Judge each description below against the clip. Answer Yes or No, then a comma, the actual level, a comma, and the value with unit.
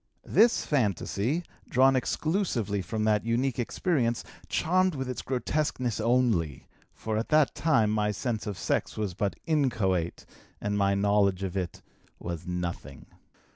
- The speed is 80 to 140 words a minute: Yes, slow, 135 wpm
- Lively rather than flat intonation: No, average, 5.0 semitones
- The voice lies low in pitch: Yes, low, 110 Hz